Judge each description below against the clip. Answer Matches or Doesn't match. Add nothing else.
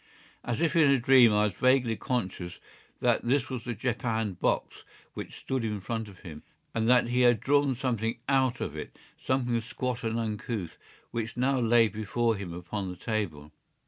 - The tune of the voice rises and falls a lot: Doesn't match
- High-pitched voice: Doesn't match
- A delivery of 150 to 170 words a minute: Doesn't match